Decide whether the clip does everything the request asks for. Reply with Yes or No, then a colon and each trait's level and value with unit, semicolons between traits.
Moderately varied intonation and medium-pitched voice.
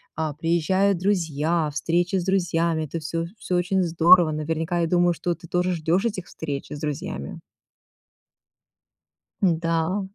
No: narrow, 2.0 semitones; medium, 170 Hz